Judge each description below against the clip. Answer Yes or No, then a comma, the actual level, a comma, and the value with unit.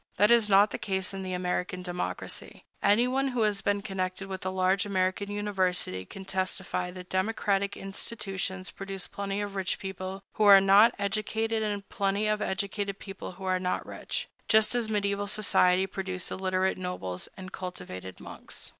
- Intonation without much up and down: Yes, narrow, 1.6 semitones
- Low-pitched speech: No, high, 195 Hz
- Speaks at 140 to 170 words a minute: Yes, average, 165 wpm